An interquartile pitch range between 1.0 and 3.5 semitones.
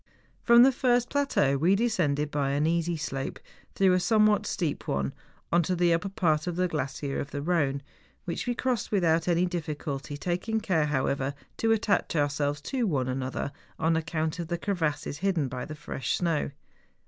No: average, 4.4 semitones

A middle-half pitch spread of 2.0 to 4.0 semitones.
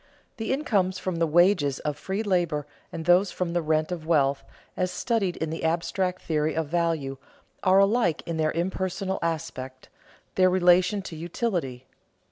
Yes: average, 3.1 semitones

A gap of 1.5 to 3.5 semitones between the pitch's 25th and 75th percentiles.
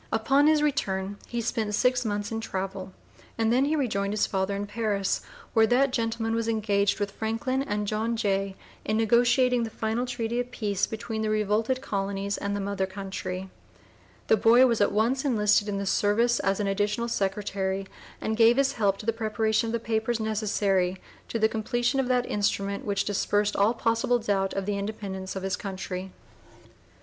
Yes: average, 2.7 semitones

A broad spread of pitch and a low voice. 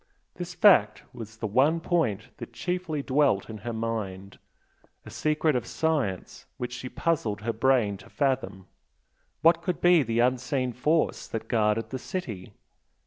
Yes: wide, 5.8 semitones; low, 125 Hz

